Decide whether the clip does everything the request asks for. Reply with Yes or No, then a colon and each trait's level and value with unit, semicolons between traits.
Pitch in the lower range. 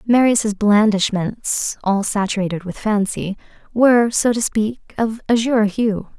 No: high, 215 Hz